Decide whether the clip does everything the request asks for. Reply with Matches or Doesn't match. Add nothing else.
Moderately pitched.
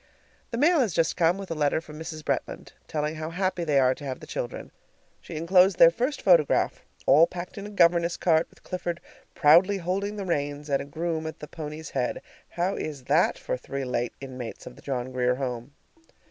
Matches